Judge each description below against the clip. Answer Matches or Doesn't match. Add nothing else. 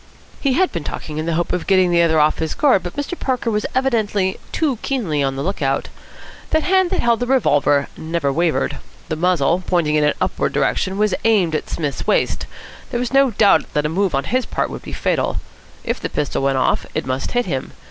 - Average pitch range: Doesn't match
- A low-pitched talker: Doesn't match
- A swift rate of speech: Matches